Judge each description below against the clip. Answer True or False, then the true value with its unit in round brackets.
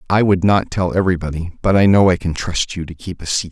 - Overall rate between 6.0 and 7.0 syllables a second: True (6.3 syllables/s)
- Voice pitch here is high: False (90 Hz)